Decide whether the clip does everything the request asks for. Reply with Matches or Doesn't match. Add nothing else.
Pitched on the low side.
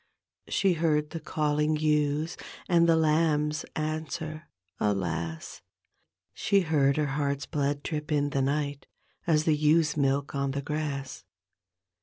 Doesn't match